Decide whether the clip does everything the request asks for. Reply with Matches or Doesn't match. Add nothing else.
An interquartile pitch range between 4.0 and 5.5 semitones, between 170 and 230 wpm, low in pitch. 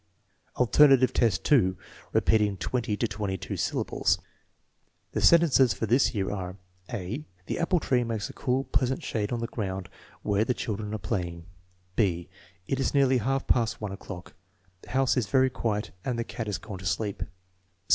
Matches